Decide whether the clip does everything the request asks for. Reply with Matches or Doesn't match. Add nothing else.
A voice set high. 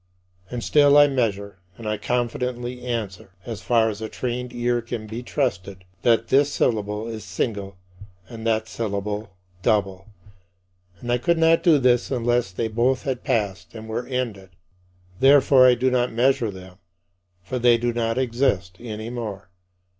Doesn't match